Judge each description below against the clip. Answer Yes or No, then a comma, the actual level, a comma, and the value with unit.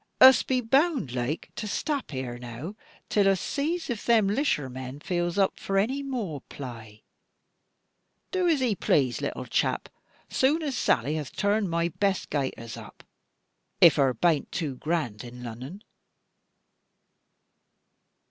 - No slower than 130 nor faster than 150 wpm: Yes, average, 140 wpm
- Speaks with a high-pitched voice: No, medium, 175 Hz